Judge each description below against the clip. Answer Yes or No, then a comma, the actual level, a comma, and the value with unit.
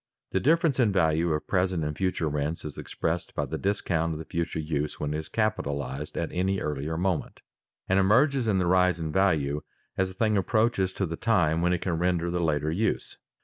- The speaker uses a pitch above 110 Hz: No, very low, 85 Hz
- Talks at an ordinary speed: No, fast, 215 wpm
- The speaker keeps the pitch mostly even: No, average, 3.7 semitones